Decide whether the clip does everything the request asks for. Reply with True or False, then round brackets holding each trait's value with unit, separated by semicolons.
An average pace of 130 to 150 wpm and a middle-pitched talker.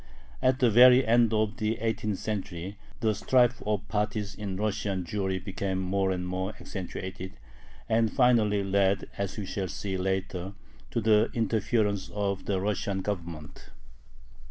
False (145 wpm; 100 Hz)